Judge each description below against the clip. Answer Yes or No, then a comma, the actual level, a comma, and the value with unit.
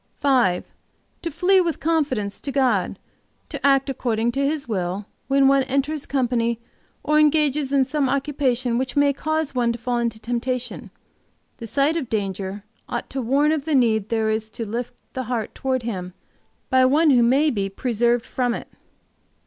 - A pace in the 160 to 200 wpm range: Yes, average, 175 wpm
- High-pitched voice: Yes, very high, 255 Hz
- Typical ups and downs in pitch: Yes, average, 3.4 semitones